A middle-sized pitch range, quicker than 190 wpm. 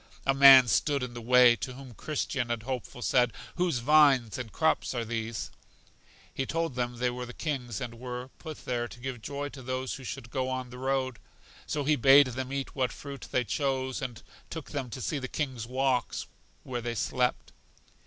No: narrow, 2.0 semitones; average, 200 wpm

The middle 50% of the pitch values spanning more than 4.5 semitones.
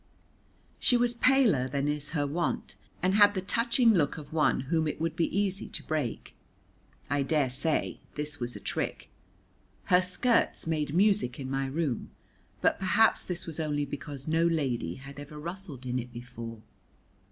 Yes: average, 5.1 semitones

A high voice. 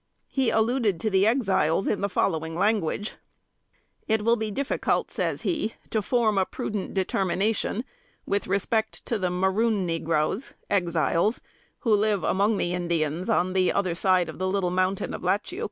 Yes: high, 195 Hz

